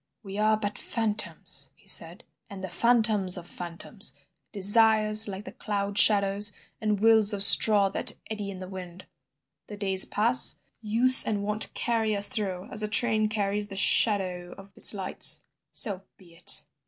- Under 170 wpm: Yes, average, 155 wpm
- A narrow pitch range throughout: Yes, narrow, 1.9 semitones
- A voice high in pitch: Yes, high, 205 Hz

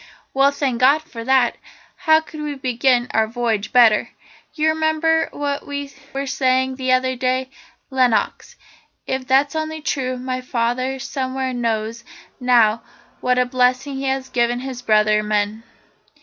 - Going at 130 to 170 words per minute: Yes, average, 150 wpm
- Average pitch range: No, narrow, 2.2 semitones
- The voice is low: No, very high, 255 Hz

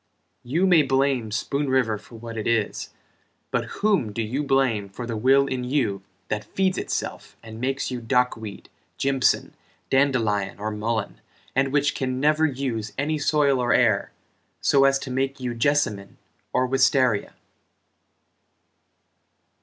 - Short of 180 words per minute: Yes, average, 145 wpm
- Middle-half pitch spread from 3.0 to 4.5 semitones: Yes, average, 3.6 semitones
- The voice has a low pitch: Yes, low, 130 Hz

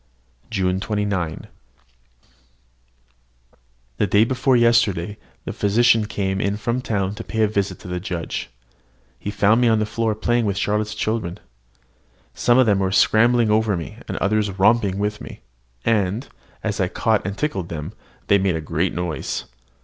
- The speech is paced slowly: No, average, 160 wpm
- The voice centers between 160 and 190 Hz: No, low, 105 Hz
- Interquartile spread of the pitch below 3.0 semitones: Yes, narrow, 2.6 semitones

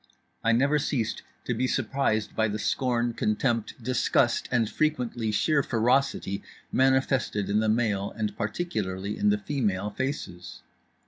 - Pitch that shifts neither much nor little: Yes, average, 4.0 semitones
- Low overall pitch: Yes, low, 115 Hz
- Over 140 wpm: No, slow, 135 wpm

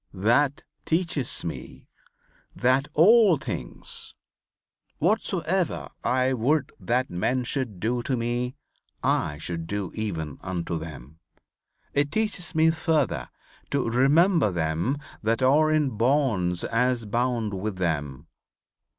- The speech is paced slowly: Yes, slow, 115 wpm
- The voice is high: No, low, 125 Hz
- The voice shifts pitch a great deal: Yes, wide, 7.9 semitones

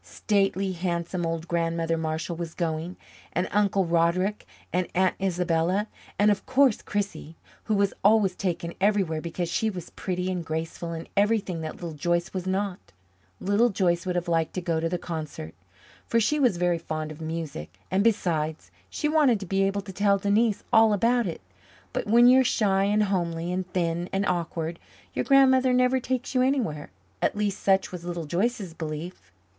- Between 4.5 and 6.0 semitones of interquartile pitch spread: No, average, 3.6 semitones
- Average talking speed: Yes, average, 180 wpm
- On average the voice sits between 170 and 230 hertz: Yes, medium, 185 Hz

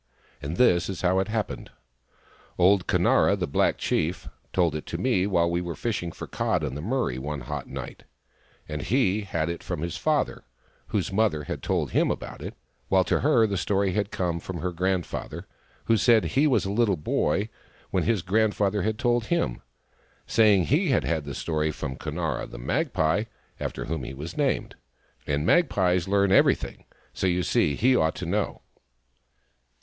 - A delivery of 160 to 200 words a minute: Yes, average, 185 wpm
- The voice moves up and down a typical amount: Yes, average, 4.5 semitones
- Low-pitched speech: Yes, very low, 95 Hz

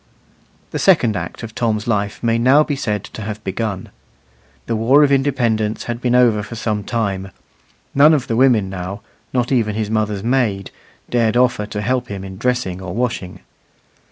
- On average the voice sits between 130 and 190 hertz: No, low, 110 Hz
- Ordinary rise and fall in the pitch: Yes, average, 3.3 semitones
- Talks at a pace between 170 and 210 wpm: Yes, average, 180 wpm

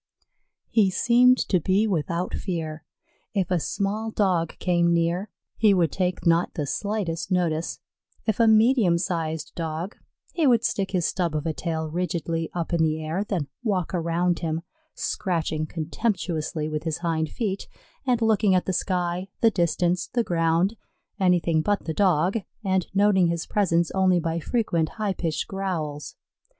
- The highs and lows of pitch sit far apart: No, average, 3.2 semitones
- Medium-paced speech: Yes, average, 160 wpm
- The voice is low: No, medium, 175 Hz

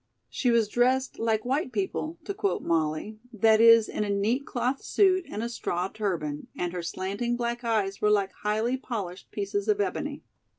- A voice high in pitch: Yes, high, 225 Hz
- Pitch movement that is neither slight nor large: Yes, average, 4.1 semitones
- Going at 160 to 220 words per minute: Yes, average, 180 wpm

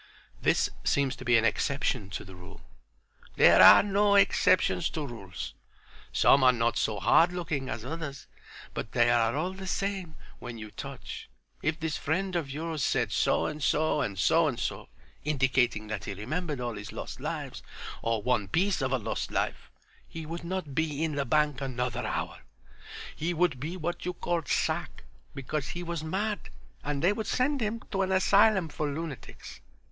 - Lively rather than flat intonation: Yes, wide, 6.1 semitones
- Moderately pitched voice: Yes, medium, 150 Hz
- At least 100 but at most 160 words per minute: No, average, 180 wpm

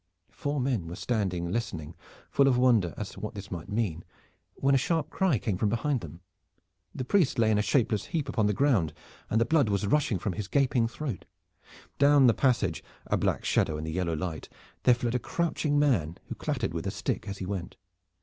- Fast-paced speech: Yes, fast, 215 wpm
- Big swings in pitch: Yes, wide, 6.5 semitones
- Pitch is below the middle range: Yes, low, 110 Hz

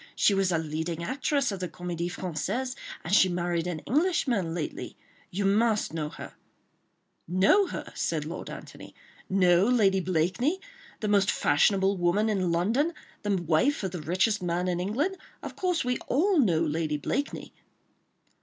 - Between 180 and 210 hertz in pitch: Yes, high, 190 Hz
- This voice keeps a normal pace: Yes, average, 150 wpm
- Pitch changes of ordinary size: No, wide, 5.9 semitones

